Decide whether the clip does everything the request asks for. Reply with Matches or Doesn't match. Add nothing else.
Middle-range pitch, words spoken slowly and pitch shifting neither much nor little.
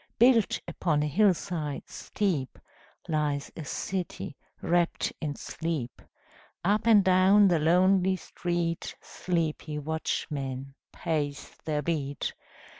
Matches